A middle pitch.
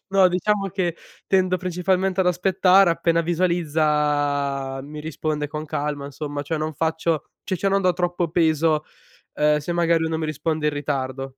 Yes: medium, 160 Hz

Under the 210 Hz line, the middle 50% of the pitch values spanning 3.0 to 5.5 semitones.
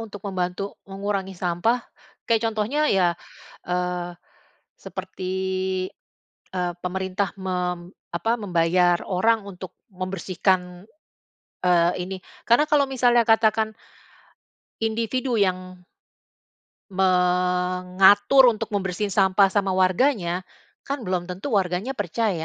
Yes: high, 190 Hz; average, 3.3 semitones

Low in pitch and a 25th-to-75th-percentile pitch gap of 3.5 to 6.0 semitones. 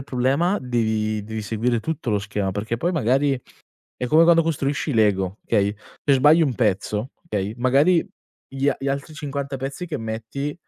Yes: low, 130 Hz; average, 4.9 semitones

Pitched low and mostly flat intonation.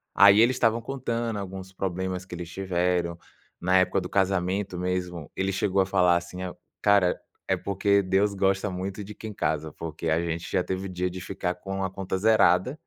Yes: very low, 95 Hz; narrow, 1.8 semitones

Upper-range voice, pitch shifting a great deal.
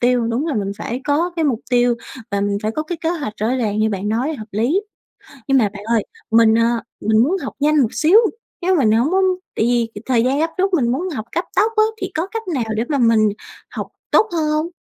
Yes: high, 245 Hz; wide, 6.0 semitones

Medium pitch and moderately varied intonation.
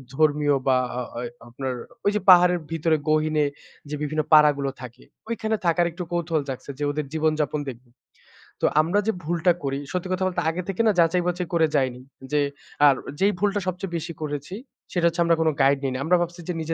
Yes: medium, 160 Hz; average, 3.4 semitones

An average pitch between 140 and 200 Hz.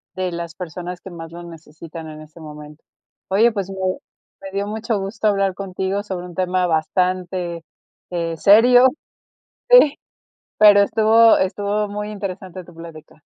Yes: medium, 185 Hz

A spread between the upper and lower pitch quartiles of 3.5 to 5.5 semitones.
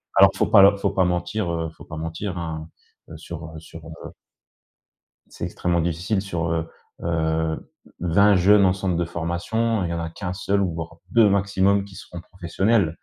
No: average, 3.1 semitones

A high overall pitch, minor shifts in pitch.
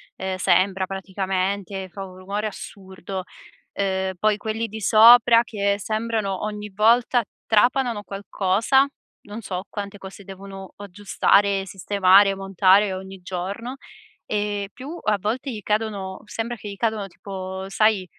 Yes: high, 200 Hz; narrow, 2.1 semitones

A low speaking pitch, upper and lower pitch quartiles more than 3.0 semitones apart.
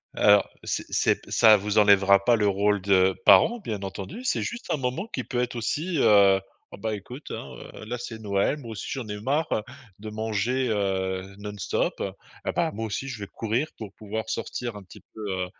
Yes: low, 105 Hz; average, 3.5 semitones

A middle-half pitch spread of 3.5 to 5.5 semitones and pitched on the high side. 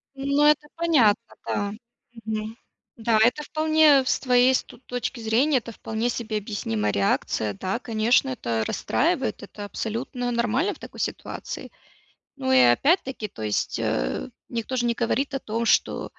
Yes: average, 3.8 semitones; high, 235 Hz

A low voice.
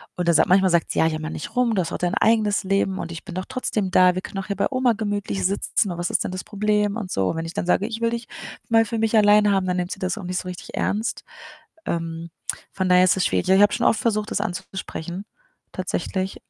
No: high, 195 Hz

